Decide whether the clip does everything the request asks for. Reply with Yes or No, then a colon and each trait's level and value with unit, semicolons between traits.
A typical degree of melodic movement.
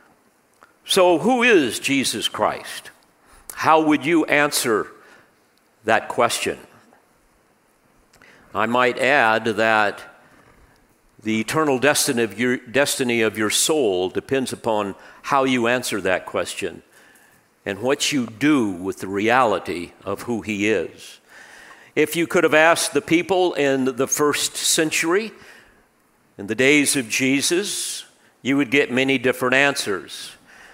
Yes: average, 4.7 semitones